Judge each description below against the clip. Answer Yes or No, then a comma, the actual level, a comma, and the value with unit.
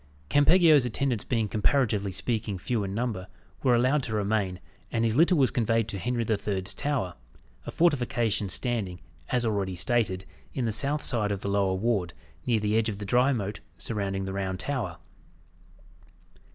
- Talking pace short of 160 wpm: No, average, 170 wpm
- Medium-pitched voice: No, low, 110 Hz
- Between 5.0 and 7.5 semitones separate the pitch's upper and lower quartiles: No, average, 3.9 semitones